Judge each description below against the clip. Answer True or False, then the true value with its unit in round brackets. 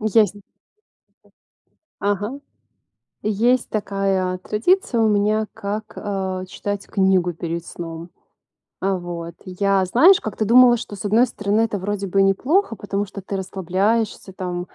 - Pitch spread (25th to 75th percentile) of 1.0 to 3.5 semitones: True (2.6 semitones)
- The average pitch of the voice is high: True (200 Hz)